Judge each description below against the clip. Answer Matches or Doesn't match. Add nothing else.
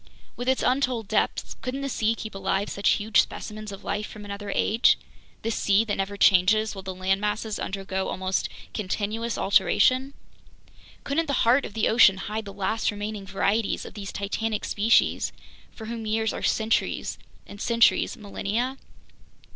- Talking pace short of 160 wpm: Doesn't match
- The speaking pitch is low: Doesn't match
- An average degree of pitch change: Doesn't match